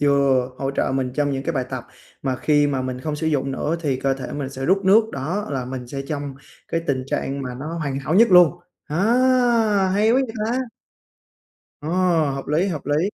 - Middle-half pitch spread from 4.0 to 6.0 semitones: No, average, 3.6 semitones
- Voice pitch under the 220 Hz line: Yes, medium, 140 Hz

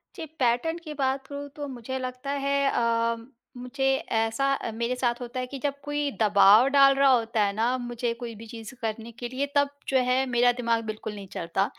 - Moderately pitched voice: No, high, 245 Hz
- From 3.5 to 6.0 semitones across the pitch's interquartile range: No, average, 3.1 semitones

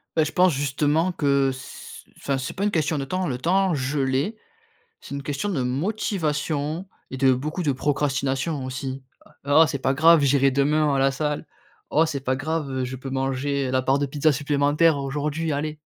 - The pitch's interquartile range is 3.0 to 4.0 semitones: No, narrow, 2.6 semitones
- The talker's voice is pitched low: No, medium, 145 Hz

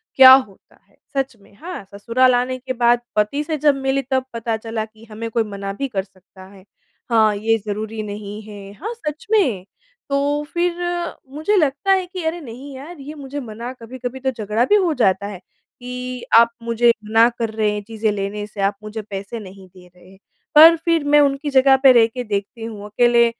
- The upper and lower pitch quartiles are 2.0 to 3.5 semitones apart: No, average, 4.5 semitones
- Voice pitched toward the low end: No, high, 235 Hz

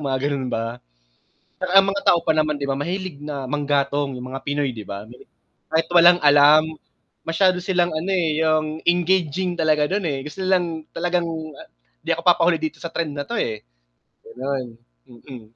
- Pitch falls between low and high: Yes, medium, 155 Hz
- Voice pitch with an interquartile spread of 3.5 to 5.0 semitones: Yes, average, 3.8 semitones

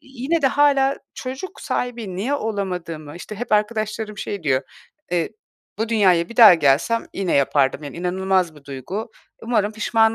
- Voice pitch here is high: Yes, high, 210 Hz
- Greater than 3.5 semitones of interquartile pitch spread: Yes, wide, 5.5 semitones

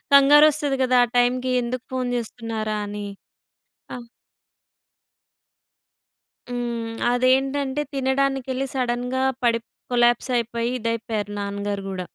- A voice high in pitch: Yes, high, 245 Hz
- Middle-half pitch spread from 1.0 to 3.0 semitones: Yes, narrow, 2.5 semitones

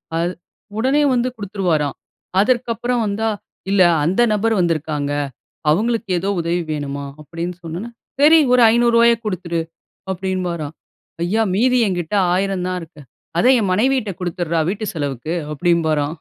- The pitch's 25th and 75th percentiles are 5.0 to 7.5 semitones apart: Yes, average, 5.3 semitones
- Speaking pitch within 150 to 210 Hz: Yes, medium, 185 Hz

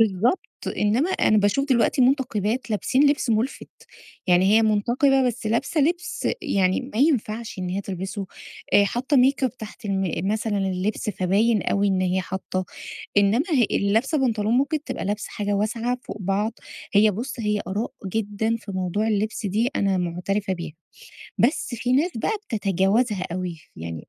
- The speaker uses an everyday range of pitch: Yes, average, 4.1 semitones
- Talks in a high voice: Yes, high, 215 Hz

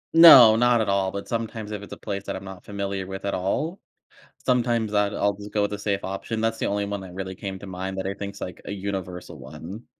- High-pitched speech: No, low, 100 Hz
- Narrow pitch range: Yes, narrow, 2.3 semitones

